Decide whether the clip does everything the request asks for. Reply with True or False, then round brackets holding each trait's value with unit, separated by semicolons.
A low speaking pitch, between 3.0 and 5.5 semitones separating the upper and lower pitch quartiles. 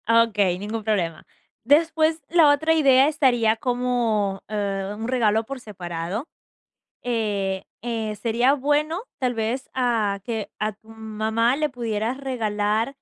False (230 Hz; 3.7 semitones)